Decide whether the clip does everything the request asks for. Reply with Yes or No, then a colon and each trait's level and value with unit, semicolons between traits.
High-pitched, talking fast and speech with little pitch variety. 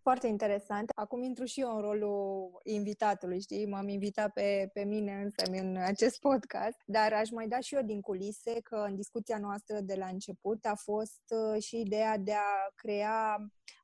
Yes: high, 210 Hz; fast, 180 wpm; narrow, 1.7 semitones